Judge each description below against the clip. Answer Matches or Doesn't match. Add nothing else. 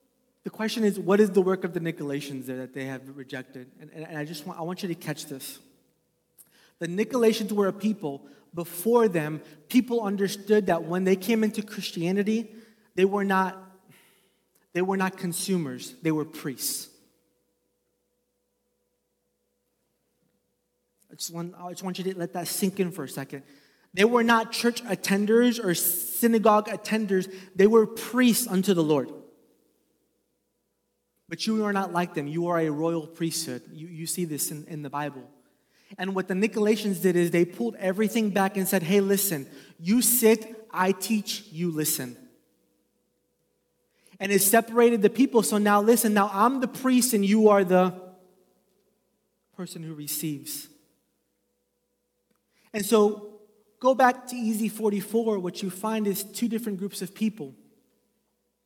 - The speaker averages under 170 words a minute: Matches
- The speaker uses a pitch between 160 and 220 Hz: Matches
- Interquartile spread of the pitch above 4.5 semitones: Matches